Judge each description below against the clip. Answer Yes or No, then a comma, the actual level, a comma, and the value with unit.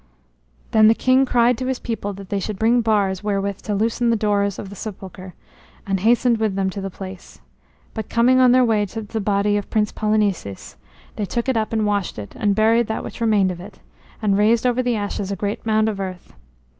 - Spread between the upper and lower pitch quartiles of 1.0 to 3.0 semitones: Yes, narrow, 2.5 semitones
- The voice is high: Yes, high, 210 Hz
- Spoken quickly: Yes, fast, 220 wpm